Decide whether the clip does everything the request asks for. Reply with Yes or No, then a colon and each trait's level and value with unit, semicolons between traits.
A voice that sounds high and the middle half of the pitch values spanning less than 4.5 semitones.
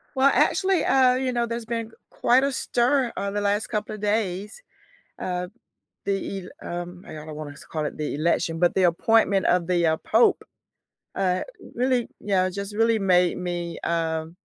No: high, 200 Hz; average, 4.8 semitones